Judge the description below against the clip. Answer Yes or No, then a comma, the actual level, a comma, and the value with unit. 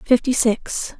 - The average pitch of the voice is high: Yes, high, 240 Hz